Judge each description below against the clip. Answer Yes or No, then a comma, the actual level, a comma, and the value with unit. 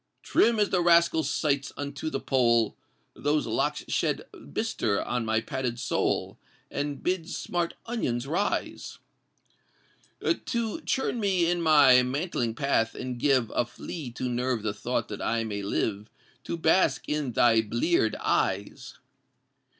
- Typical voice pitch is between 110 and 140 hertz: Yes, low, 135 Hz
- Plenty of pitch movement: Yes, wide, 6.3 semitones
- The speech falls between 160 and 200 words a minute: No, average, 140 wpm